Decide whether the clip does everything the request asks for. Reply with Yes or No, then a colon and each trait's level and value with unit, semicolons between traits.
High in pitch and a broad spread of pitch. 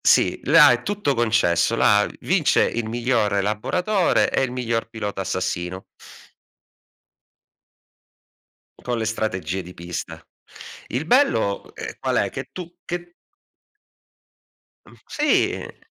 No: low, 115 Hz; wide, 7.8 semitones